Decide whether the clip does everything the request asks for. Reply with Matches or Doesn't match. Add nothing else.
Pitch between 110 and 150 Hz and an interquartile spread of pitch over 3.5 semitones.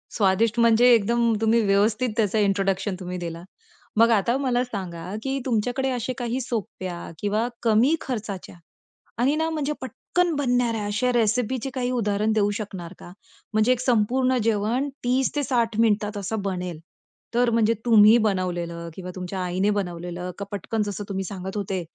Doesn't match